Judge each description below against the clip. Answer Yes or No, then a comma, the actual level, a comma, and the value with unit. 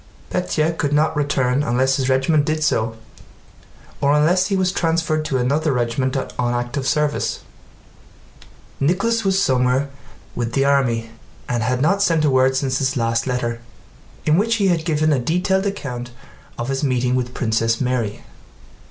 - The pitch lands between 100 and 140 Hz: Yes, low, 135 Hz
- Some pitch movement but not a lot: Yes, average, 4.0 semitones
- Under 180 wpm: Yes, average, 160 wpm